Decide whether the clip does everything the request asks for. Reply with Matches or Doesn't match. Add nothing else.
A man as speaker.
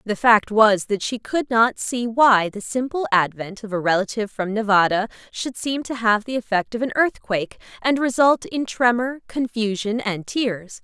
Doesn't match